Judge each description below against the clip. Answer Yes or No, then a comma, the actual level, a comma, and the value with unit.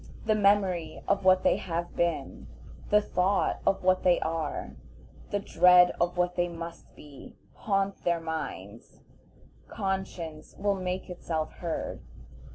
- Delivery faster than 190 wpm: No, slow, 135 wpm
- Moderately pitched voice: Yes, medium, 180 Hz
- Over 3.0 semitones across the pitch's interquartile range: No, average, 2.7 semitones